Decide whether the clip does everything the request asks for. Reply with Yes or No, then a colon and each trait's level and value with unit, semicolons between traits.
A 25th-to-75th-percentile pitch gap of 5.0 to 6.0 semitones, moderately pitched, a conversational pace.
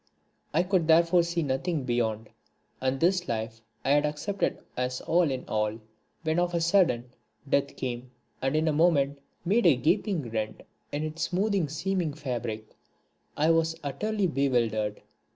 Yes: average, 5.3 semitones; medium, 150 Hz; average, 150 wpm